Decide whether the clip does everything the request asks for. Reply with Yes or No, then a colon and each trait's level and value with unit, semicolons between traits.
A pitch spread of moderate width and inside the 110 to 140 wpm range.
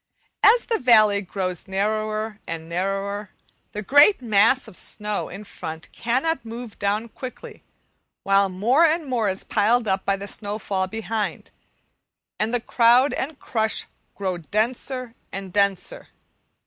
Yes: average, 3.6 semitones; slow, 135 wpm